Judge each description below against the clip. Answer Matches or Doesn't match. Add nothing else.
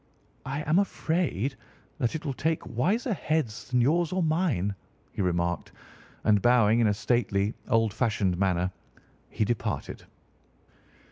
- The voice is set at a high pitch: Doesn't match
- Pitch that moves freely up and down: Matches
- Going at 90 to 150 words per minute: Matches